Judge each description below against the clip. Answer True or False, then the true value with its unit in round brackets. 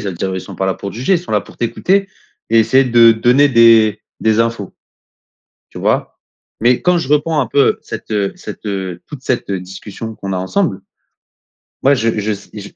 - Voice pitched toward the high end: False (115 Hz)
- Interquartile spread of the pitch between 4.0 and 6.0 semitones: True (4.8 semitones)